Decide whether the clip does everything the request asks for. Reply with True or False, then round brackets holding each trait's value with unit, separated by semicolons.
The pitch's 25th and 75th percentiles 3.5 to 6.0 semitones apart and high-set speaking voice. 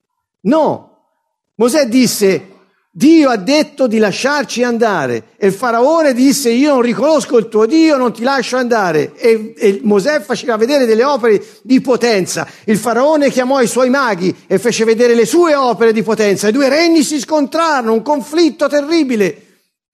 True (4.6 semitones; 245 Hz)